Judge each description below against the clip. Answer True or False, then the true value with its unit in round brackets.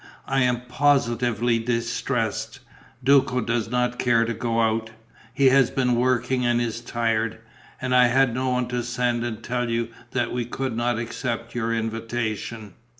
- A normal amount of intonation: False (1.4 semitones)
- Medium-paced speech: True (160 wpm)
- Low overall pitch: True (120 Hz)